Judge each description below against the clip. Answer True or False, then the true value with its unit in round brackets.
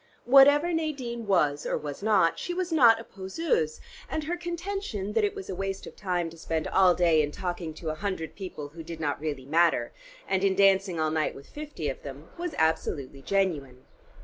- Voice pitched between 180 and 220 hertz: True (190 Hz)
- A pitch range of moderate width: False (7.9 semitones)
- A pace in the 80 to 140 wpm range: False (200 wpm)